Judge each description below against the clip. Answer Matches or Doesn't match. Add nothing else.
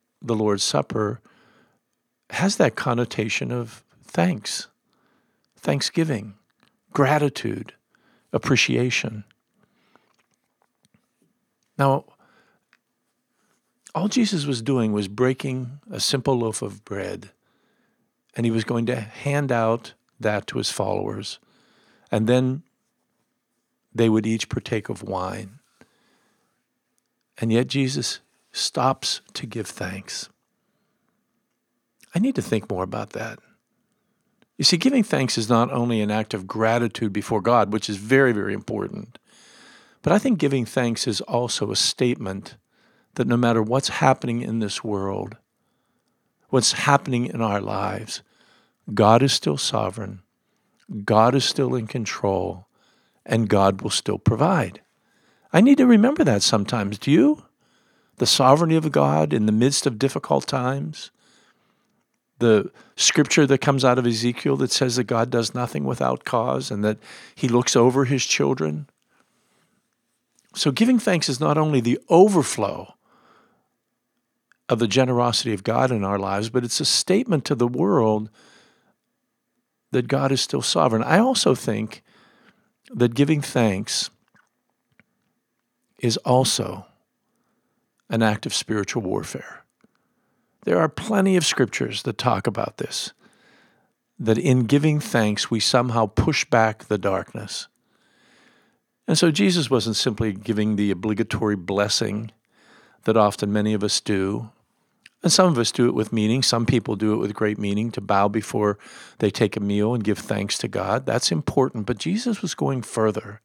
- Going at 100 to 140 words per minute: Matches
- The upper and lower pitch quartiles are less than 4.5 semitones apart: Matches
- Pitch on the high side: Doesn't match